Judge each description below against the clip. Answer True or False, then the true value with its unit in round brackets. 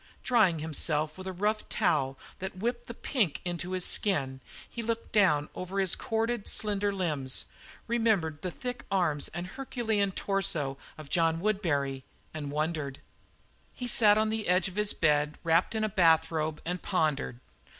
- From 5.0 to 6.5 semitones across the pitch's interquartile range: True (5.4 semitones)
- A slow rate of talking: False (160 wpm)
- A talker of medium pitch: True (180 Hz)